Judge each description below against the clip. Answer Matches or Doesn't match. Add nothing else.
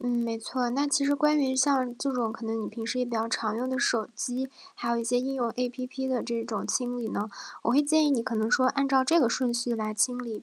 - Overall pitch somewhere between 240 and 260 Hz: Matches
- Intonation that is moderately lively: Doesn't match